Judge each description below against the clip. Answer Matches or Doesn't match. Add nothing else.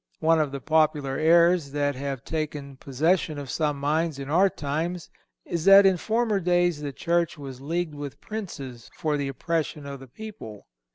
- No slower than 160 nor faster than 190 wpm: Matches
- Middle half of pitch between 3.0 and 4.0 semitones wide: Matches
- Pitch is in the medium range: Matches